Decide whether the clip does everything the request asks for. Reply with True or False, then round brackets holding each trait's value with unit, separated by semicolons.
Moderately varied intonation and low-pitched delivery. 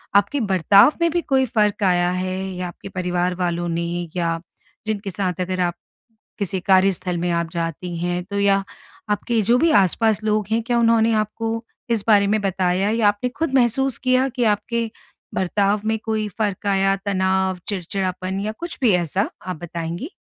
False (3.4 semitones; 200 Hz)